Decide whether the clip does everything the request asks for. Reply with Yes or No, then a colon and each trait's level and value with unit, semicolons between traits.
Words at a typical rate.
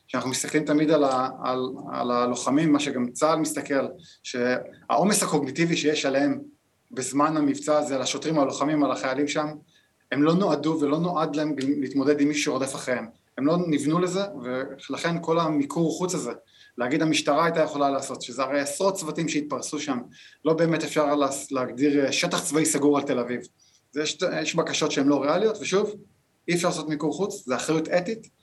No: fast, 175 wpm